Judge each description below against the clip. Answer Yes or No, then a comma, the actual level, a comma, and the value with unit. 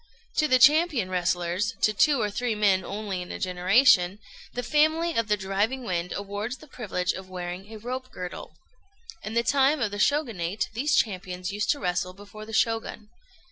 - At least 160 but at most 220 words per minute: Yes, average, 180 wpm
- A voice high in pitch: Yes, high, 210 Hz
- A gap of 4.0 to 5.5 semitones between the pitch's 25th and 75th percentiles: Yes, average, 5.2 semitones